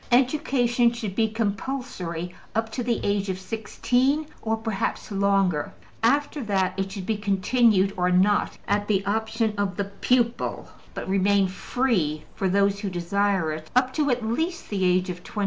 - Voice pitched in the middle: No, high, 205 Hz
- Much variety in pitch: No, average, 3.8 semitones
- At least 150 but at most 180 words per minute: Yes, average, 165 wpm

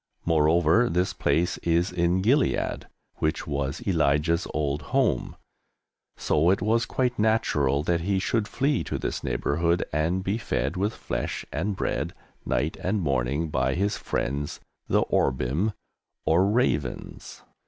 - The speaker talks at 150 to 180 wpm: No, slow, 135 wpm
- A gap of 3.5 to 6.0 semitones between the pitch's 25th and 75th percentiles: Yes, average, 5.2 semitones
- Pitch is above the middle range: No, very low, 85 Hz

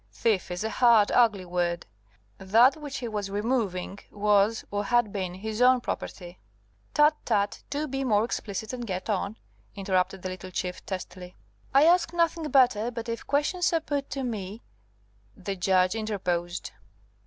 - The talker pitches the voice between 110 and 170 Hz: No, high, 210 Hz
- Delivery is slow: No, average, 165 wpm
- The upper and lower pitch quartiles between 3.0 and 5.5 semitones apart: Yes, average, 5.0 semitones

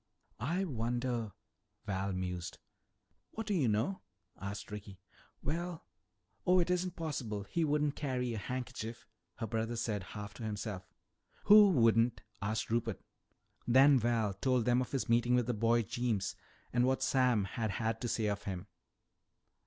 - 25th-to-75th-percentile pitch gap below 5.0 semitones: Yes, average, 3.9 semitones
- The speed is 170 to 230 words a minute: No, average, 155 wpm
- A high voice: No, low, 120 Hz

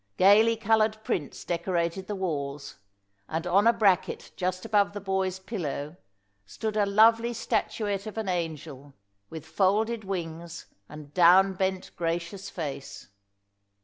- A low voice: No, high, 190 Hz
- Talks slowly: Yes, slow, 130 wpm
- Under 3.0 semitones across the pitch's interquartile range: No, average, 3.8 semitones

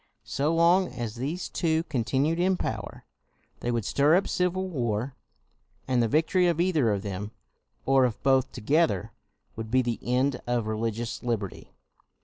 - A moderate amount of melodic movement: No, wide, 6.2 semitones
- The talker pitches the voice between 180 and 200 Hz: No, low, 130 Hz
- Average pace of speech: Yes, average, 155 wpm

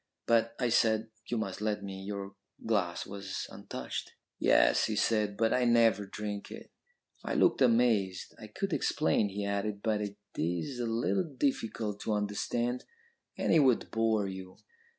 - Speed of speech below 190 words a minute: Yes, average, 160 wpm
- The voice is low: Yes, low, 105 Hz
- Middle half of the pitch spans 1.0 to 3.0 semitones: Yes, narrow, 2.5 semitones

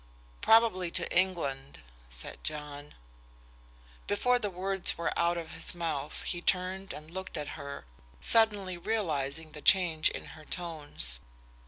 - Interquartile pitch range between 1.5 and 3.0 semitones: No, average, 4.1 semitones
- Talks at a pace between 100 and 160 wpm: Yes, slow, 135 wpm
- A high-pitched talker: No, medium, 170 Hz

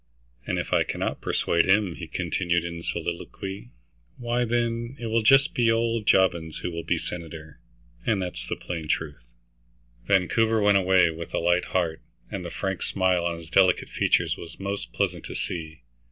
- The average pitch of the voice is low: Yes, very low, 90 Hz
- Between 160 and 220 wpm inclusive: Yes, average, 175 wpm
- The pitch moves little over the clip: No, average, 4.3 semitones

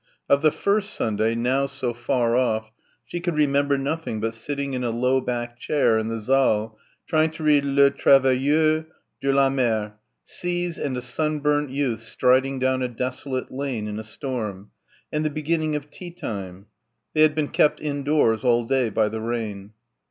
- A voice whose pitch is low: Yes, low, 130 Hz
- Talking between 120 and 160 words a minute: No, average, 175 wpm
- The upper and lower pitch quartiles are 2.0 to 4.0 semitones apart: No, average, 4.4 semitones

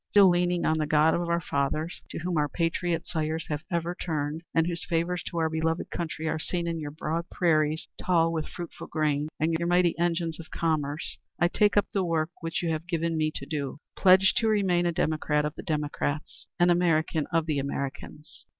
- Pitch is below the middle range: No, medium, 165 Hz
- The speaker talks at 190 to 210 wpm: Yes, fast, 205 wpm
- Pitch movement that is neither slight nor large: No, narrow, 2.0 semitones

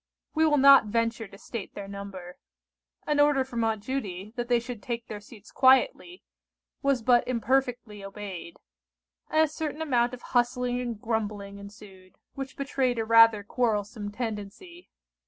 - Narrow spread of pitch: No, average, 4.1 semitones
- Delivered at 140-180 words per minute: Yes, average, 155 wpm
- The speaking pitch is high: Yes, high, 235 Hz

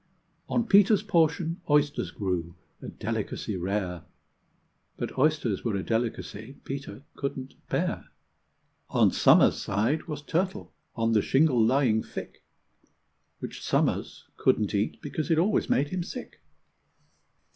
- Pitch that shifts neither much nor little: No, wide, 7.0 semitones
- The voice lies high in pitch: No, low, 135 Hz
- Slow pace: Yes, slow, 125 wpm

